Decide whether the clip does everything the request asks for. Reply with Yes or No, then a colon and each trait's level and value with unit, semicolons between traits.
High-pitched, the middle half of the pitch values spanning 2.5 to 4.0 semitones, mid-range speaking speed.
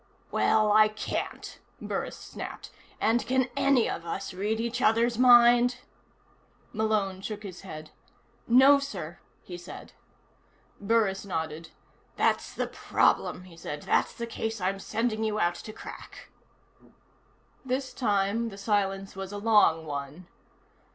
No: high, 210 Hz; average, 3.7 semitones; slow, 130 wpm